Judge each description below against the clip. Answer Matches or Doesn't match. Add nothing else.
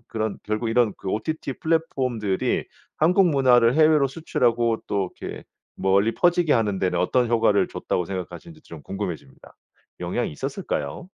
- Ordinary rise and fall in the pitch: Doesn't match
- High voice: Doesn't match